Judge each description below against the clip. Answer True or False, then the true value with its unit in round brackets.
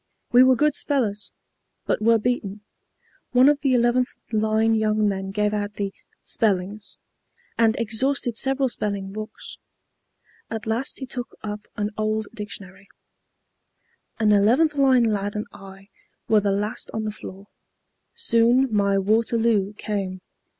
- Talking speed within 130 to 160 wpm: True (135 wpm)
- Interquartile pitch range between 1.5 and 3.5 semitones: True (2.8 semitones)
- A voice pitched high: True (215 Hz)